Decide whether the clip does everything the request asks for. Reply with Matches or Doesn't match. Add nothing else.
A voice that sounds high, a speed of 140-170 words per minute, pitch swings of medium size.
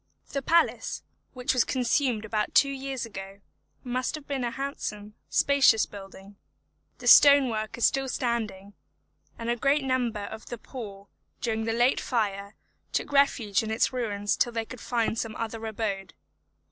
Matches